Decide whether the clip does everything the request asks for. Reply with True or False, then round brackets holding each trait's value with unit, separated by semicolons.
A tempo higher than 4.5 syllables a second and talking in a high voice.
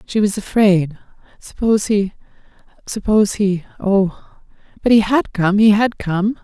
False (4.3 syllables/s; 205 Hz)